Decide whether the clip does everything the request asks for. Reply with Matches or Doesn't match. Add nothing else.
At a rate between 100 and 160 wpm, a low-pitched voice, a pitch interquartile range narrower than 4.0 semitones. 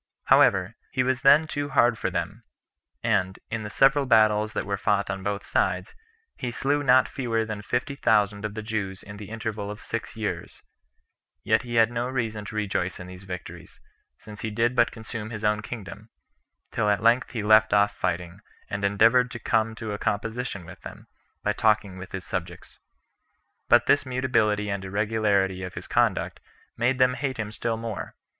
Doesn't match